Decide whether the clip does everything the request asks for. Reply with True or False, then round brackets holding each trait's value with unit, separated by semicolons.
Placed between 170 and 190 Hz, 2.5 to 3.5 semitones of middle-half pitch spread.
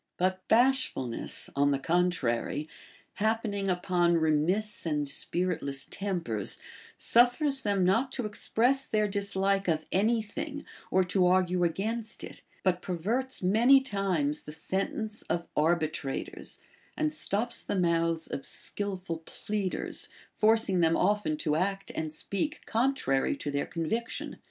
False (185 Hz; 4.9 semitones)